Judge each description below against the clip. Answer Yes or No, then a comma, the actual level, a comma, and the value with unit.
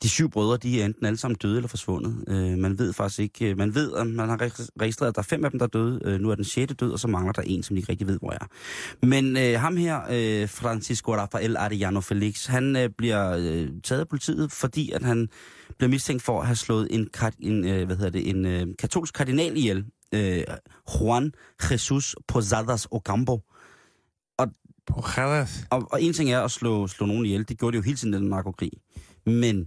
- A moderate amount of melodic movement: Yes, average, 3.7 semitones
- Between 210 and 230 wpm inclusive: Yes, average, 220 wpm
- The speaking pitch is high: No, low, 115 Hz